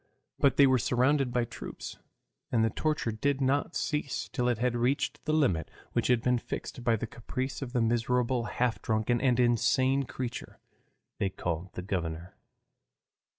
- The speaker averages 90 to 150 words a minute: No, average, 165 wpm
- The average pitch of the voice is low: Yes, low, 125 Hz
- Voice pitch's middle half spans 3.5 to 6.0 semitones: No, average, 2.8 semitones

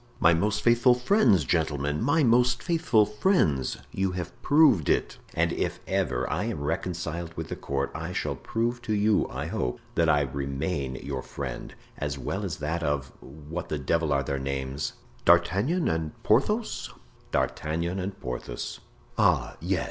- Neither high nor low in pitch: No, very low, 85 Hz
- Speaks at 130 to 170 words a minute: Yes, average, 155 wpm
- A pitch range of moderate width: No, wide, 7.0 semitones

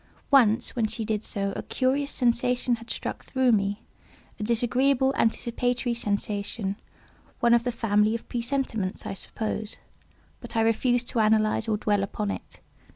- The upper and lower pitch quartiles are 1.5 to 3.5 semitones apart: Yes, narrow, 2.6 semitones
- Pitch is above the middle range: Yes, high, 230 Hz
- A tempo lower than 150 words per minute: Yes, average, 140 wpm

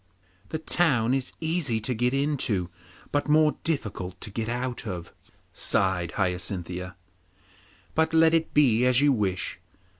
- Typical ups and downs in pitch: No, wide, 7.8 semitones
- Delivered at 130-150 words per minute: Yes, average, 140 wpm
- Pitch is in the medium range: No, low, 125 Hz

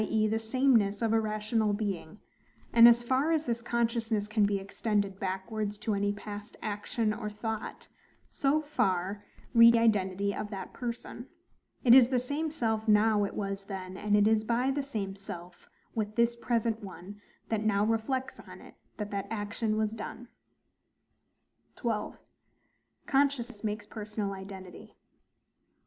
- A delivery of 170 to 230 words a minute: No, average, 155 wpm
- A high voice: Yes, high, 215 Hz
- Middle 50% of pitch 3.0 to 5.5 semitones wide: No, narrow, 2.5 semitones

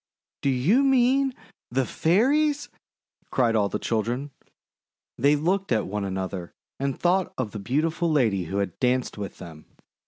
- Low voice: Yes, low, 130 Hz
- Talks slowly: No, average, 150 wpm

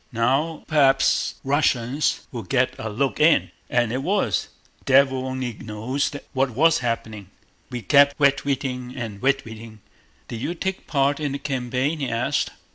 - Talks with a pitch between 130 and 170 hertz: Yes, low, 135 Hz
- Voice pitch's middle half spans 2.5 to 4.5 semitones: Yes, average, 2.9 semitones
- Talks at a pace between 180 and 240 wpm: No, average, 145 wpm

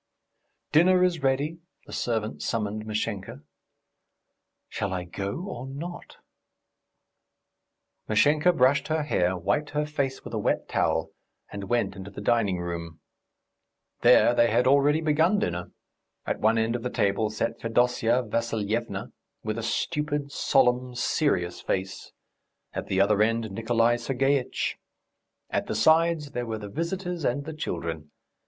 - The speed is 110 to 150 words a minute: Yes, average, 140 wpm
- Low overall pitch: Yes, low, 120 Hz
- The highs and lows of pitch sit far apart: Yes, wide, 5.7 semitones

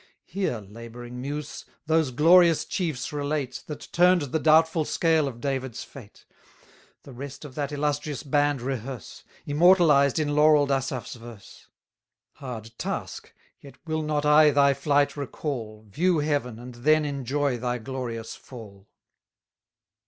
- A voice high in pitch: No, medium, 140 Hz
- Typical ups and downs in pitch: Yes, average, 3.5 semitones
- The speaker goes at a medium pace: No, slow, 130 wpm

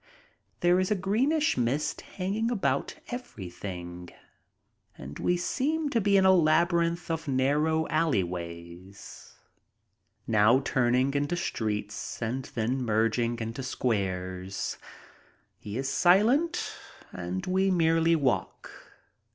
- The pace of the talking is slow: Yes, slow, 110 wpm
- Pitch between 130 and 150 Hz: Yes, low, 135 Hz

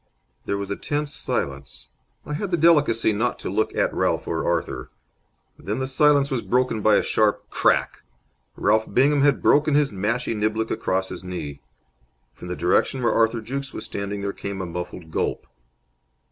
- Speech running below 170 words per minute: No, average, 175 wpm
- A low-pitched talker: Yes, low, 110 Hz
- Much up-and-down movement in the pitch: Yes, wide, 5.7 semitones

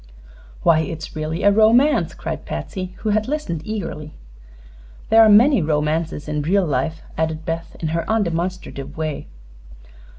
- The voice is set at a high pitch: No, medium, 165 Hz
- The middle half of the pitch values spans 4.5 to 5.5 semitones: Yes, average, 5.1 semitones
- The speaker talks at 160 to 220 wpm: No, average, 140 wpm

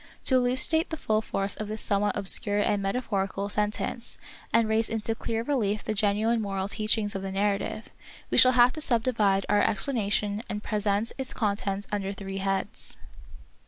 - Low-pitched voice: No, high, 210 Hz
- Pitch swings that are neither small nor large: No, narrow, 2.3 semitones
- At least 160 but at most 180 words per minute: Yes, average, 175 wpm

